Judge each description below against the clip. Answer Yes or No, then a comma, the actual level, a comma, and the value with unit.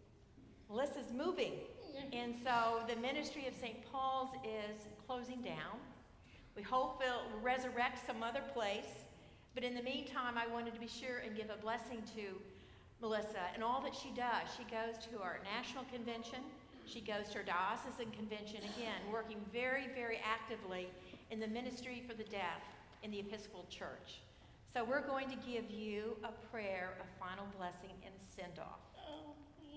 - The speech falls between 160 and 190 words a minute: Yes, average, 165 wpm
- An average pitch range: Yes, average, 3.0 semitones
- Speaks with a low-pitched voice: No, high, 235 Hz